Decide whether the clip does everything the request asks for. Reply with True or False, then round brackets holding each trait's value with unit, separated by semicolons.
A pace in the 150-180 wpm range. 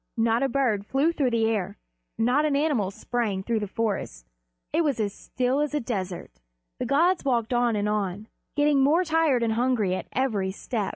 False (190 wpm)